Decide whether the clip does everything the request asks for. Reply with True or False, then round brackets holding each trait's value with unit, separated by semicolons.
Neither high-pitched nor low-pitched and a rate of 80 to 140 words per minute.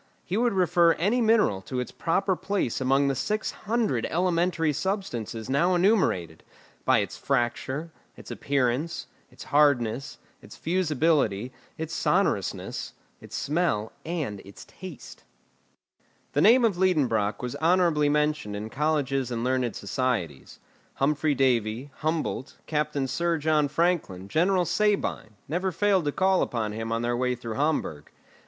True (150 Hz; 135 wpm)